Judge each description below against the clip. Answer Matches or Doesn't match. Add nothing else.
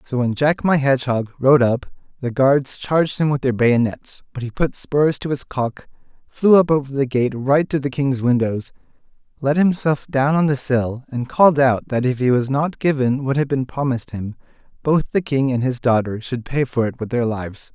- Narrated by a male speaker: Matches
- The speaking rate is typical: Doesn't match